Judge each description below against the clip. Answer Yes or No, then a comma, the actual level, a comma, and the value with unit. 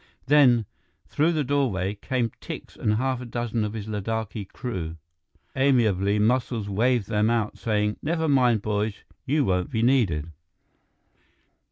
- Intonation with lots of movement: No, average, 3.7 semitones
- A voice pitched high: No, low, 115 Hz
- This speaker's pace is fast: No, average, 140 wpm